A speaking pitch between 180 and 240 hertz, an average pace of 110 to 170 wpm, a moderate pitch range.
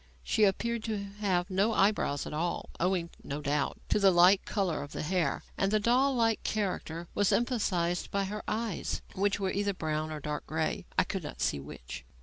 No: high, 190 Hz; average, 195 wpm; average, 4.8 semitones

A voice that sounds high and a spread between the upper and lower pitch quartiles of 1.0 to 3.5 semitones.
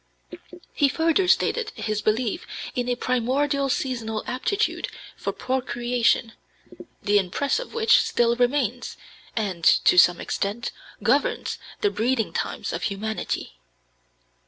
No: high, 245 Hz; average, 4.2 semitones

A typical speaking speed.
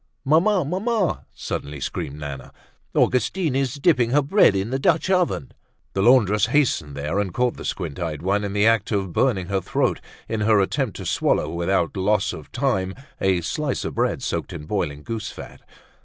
Yes: average, 185 wpm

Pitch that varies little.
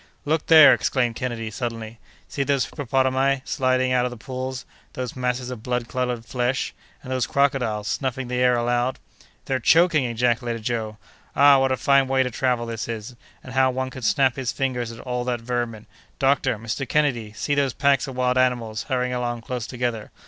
Yes: narrow, 1.9 semitones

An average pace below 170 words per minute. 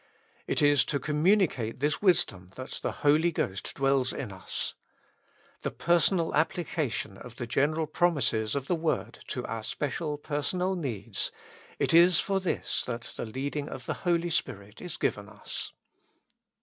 Yes: average, 155 wpm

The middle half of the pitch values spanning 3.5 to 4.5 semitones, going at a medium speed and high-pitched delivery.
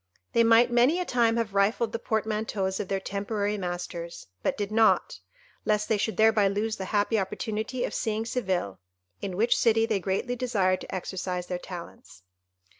No: average, 3.0 semitones; average, 175 wpm; high, 210 Hz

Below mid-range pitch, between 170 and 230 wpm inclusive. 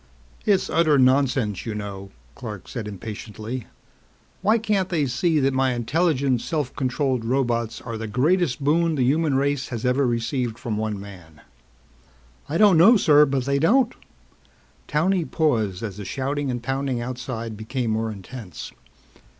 No: low, 130 Hz; average, 150 wpm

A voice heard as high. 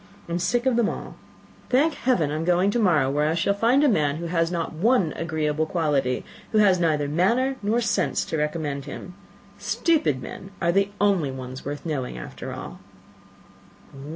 No: medium, 170 Hz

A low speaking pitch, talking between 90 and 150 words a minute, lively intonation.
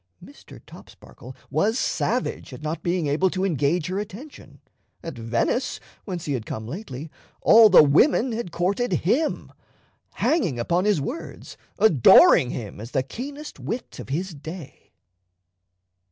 No: medium, 175 Hz; average, 140 wpm; wide, 7.7 semitones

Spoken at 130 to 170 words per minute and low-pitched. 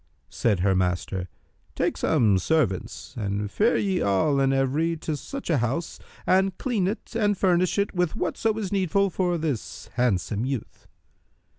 No: average, 155 wpm; medium, 155 Hz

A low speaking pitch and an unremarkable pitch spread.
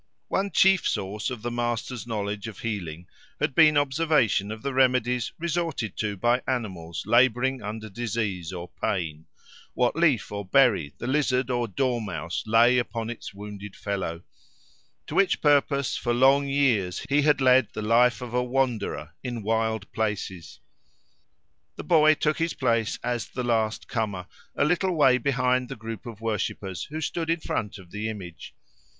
Yes: low, 120 Hz; average, 4.3 semitones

